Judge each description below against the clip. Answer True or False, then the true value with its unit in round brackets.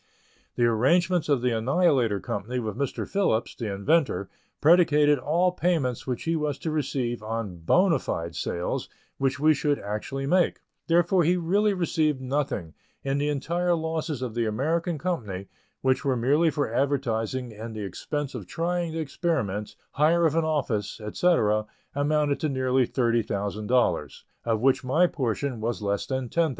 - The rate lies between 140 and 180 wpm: True (160 wpm)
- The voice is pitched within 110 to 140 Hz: True (135 Hz)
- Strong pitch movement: True (5.9 semitones)